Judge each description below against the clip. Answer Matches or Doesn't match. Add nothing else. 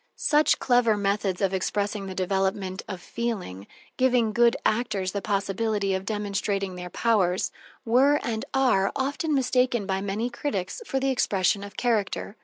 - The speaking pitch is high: Matches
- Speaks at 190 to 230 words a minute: Doesn't match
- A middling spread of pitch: Matches